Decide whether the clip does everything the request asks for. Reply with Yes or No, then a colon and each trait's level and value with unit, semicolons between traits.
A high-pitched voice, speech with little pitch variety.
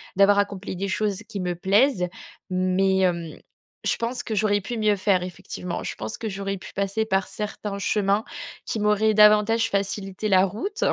Yes: high, 200 Hz; narrow, 2.0 semitones